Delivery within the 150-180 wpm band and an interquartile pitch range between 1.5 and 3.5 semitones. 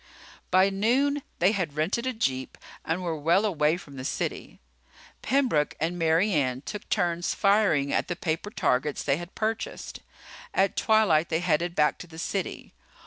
No: average, 165 wpm; average, 5.0 semitones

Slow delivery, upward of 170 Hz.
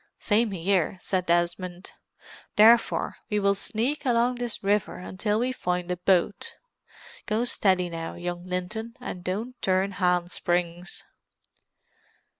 Yes: slow, 125 wpm; high, 190 Hz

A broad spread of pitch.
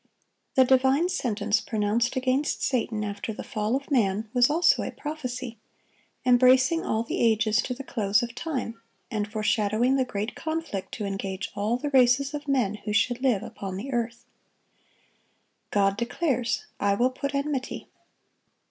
No: average, 3.9 semitones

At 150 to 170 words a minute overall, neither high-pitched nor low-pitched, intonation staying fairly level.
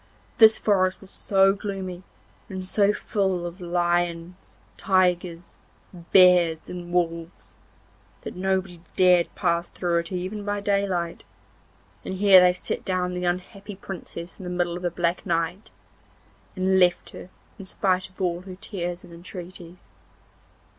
No: average, 140 wpm; medium, 180 Hz; narrow, 1.6 semitones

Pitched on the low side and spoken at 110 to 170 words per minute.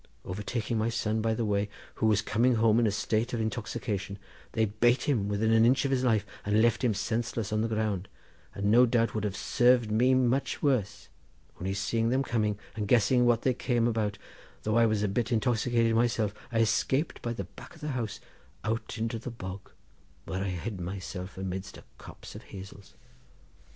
No: low, 110 Hz; average, 195 wpm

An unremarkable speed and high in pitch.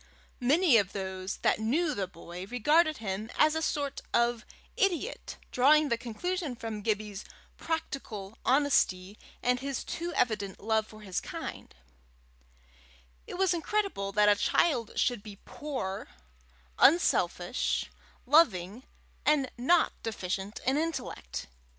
No: slow, 125 wpm; high, 240 Hz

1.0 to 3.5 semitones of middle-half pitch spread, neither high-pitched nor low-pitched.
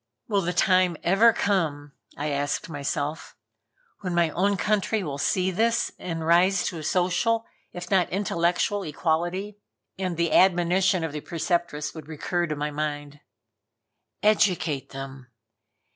No: average, 3.9 semitones; medium, 175 Hz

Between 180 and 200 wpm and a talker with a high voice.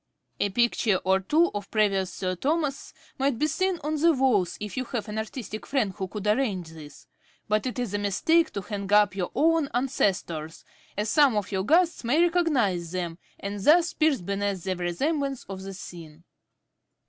Yes: average, 185 wpm; high, 210 Hz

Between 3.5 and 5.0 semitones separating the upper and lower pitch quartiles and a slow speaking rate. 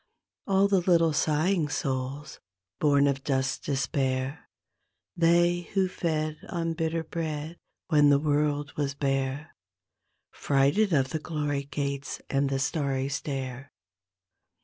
No: average, 3.0 semitones; slow, 120 wpm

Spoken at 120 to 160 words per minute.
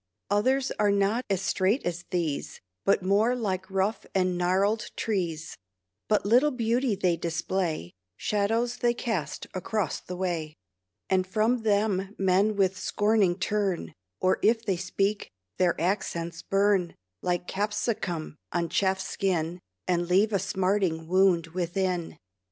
Yes: slow, 135 wpm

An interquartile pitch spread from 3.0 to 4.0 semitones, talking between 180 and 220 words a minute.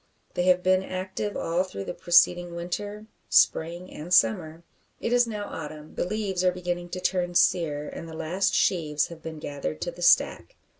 No: narrow, 2.6 semitones; average, 185 wpm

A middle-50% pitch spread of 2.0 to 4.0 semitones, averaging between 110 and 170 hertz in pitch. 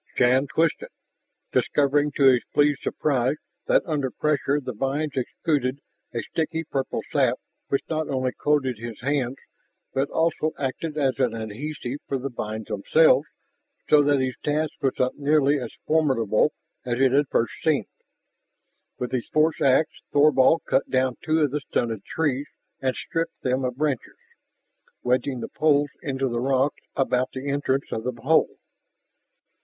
Yes: average, 2.7 semitones; low, 135 Hz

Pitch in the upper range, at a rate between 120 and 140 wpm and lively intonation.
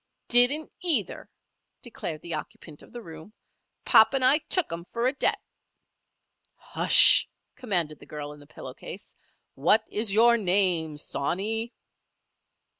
Yes: high, 205 Hz; slow, 135 wpm; wide, 7.0 semitones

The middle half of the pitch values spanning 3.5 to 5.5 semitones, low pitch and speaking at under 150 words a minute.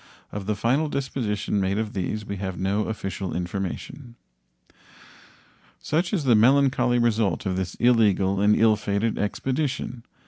Yes: average, 4.0 semitones; low, 105 Hz; average, 140 wpm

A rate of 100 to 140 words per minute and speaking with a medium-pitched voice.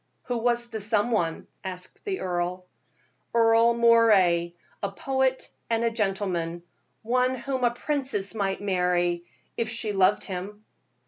No: slow, 135 wpm; high, 215 Hz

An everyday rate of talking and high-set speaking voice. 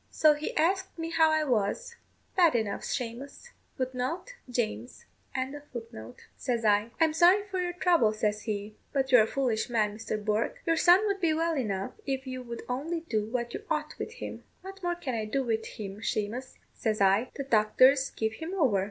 Yes: average, 180 wpm; very high, 255 Hz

